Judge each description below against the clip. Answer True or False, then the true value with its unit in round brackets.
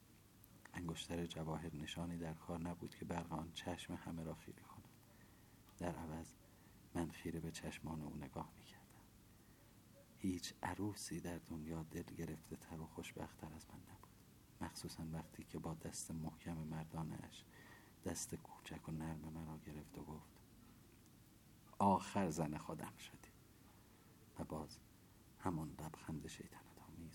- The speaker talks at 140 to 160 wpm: False (130 wpm)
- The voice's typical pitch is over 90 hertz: False (85 Hz)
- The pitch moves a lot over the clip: False (3.8 semitones)